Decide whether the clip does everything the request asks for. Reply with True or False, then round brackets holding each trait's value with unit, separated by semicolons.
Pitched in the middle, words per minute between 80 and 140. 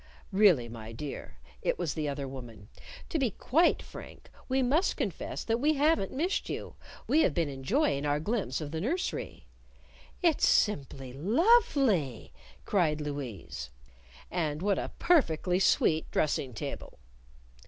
True (165 Hz; 135 wpm)